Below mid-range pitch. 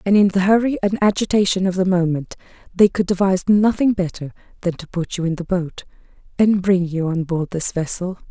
No: medium, 185 Hz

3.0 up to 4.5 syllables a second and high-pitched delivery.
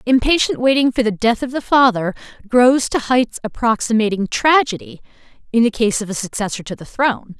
No: 5.5 syllables/s; high, 235 Hz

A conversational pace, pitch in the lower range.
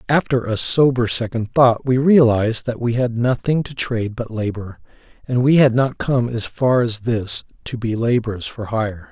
Yes: average, 190 wpm; low, 120 Hz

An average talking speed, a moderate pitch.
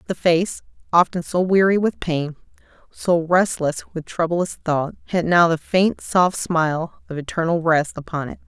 Yes: average, 165 wpm; medium, 170 Hz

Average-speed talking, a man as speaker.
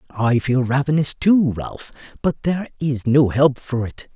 Yes: average, 175 wpm; male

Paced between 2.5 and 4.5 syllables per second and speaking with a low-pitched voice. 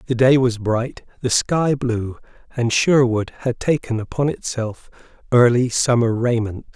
Yes: 4.2 syllables/s; low, 120 Hz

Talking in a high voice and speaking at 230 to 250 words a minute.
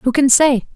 Yes: very high, 265 Hz; fast, 240 wpm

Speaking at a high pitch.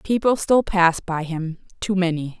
No: medium, 180 Hz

